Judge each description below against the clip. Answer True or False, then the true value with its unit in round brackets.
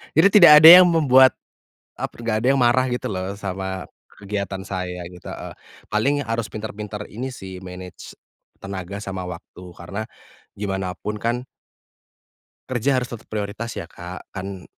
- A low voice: True (105 Hz)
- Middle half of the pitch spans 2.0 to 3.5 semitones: False (4.6 semitones)